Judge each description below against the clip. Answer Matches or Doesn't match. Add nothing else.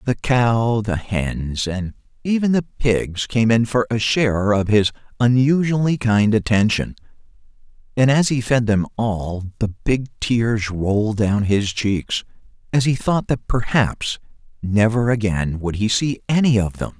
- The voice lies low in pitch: Matches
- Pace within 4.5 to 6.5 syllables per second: Doesn't match